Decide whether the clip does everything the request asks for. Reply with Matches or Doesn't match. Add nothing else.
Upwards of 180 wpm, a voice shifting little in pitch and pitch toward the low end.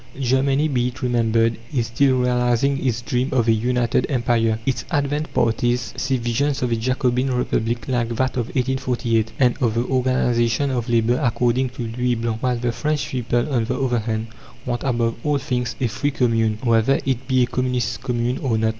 Matches